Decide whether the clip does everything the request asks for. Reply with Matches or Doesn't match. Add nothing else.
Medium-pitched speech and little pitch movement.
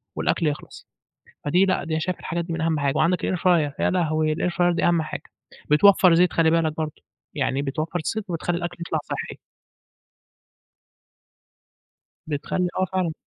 Matches